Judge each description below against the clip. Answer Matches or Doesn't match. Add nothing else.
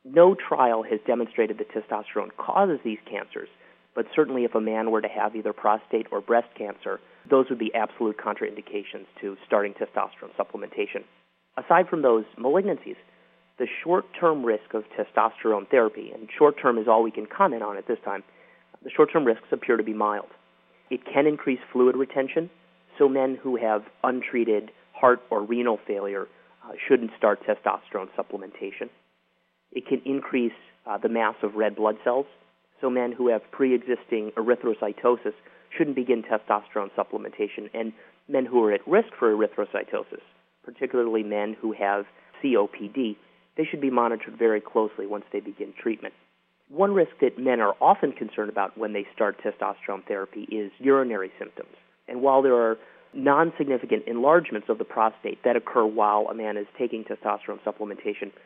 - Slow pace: Doesn't match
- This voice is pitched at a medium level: Doesn't match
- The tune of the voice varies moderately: Doesn't match